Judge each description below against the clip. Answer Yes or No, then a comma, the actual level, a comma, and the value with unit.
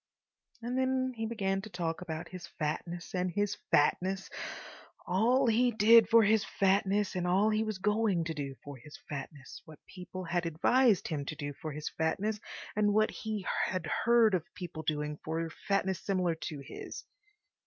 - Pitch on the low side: No, medium, 185 Hz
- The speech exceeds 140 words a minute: Yes, average, 175 wpm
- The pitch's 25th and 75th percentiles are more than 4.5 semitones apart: Yes, average, 5.0 semitones